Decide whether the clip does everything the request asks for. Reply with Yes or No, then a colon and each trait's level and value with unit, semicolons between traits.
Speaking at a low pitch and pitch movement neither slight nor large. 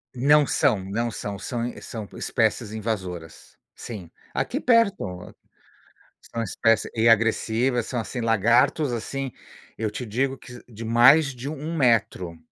Yes: low, 115 Hz; average, 3.5 semitones